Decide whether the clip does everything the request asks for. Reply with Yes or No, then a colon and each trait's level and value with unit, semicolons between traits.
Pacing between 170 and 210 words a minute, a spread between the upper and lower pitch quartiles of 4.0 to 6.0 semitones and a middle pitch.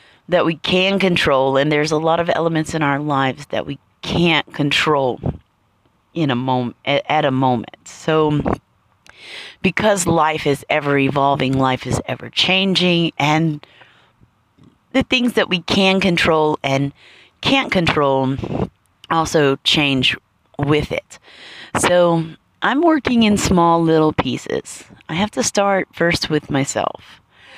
No: slow, 135 wpm; average, 4.3 semitones; medium, 155 Hz